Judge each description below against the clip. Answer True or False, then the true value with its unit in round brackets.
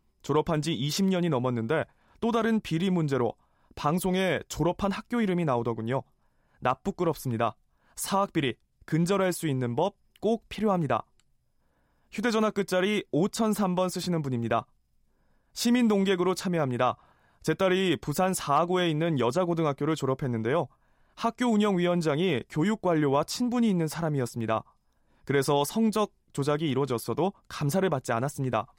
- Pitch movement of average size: False (6.2 semitones)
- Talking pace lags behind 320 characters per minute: False (325 characters per minute)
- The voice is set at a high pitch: False (165 Hz)